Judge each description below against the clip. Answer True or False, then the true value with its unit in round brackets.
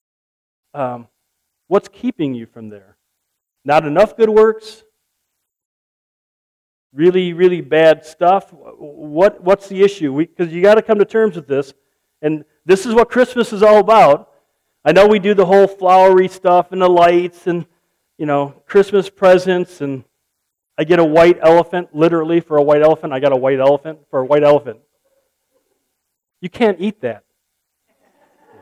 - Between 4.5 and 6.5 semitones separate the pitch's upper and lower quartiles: True (5.5 semitones)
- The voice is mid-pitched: True (175 Hz)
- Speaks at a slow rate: False (155 wpm)